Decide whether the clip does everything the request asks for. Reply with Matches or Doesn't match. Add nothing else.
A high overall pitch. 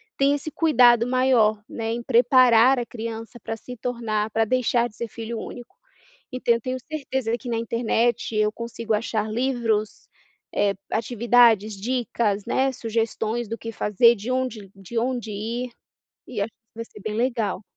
Matches